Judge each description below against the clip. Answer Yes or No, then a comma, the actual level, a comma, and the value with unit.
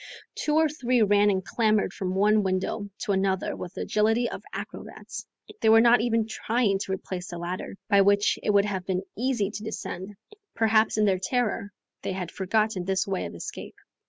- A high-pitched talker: Yes, high, 205 Hz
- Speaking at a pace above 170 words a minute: Yes, average, 190 wpm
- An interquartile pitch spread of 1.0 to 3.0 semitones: Yes, average, 2.7 semitones